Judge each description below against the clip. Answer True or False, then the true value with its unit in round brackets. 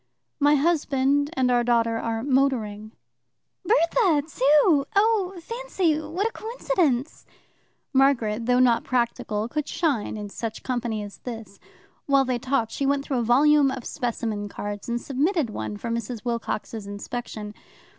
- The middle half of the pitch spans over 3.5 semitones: True (4.6 semitones)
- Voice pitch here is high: True (255 Hz)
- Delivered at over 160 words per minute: False (145 wpm)